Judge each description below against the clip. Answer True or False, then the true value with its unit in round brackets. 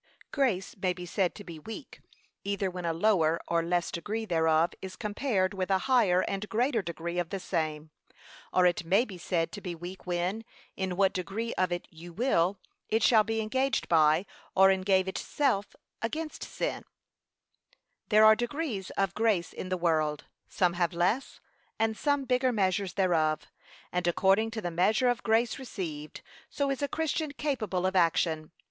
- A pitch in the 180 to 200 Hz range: True (190 Hz)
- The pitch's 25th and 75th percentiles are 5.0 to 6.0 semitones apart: False (4.3 semitones)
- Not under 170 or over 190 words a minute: True (175 wpm)